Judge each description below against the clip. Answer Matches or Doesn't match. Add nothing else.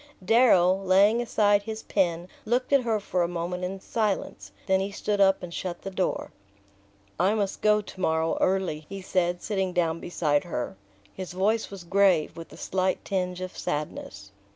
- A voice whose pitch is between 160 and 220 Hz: Matches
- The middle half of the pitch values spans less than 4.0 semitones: Matches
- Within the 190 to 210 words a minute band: Doesn't match